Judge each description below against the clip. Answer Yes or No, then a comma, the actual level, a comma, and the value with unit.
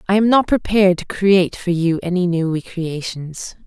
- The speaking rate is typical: Yes, average, 180 wpm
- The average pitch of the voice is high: No, medium, 180 Hz